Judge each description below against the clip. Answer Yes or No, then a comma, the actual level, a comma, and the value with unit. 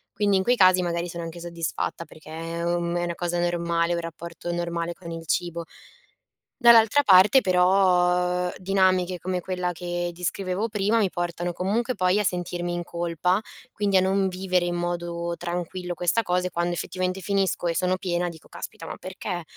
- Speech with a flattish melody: Yes, narrow, 1.5 semitones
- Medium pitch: Yes, medium, 180 Hz